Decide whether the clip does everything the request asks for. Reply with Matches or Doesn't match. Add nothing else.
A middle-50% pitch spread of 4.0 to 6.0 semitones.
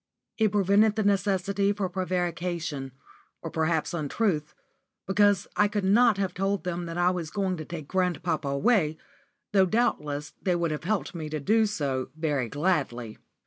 Matches